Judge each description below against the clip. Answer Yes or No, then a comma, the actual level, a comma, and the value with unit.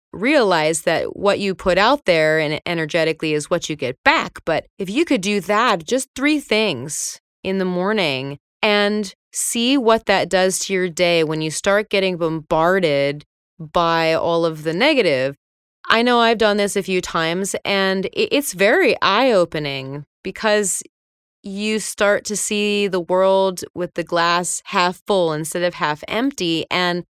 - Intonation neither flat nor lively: Yes, average, 3.9 semitones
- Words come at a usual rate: Yes, average, 165 wpm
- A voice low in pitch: No, medium, 185 Hz